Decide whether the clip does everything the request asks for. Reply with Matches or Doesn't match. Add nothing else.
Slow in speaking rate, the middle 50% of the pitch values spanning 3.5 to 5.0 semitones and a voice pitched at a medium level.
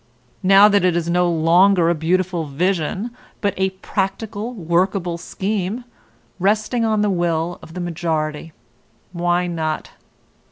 Doesn't match